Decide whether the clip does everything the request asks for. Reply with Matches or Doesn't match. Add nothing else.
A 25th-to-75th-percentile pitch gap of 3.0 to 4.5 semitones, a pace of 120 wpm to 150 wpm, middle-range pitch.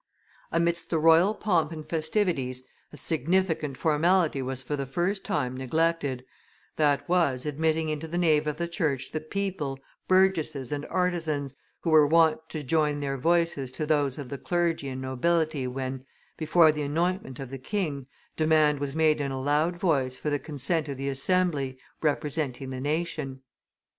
Doesn't match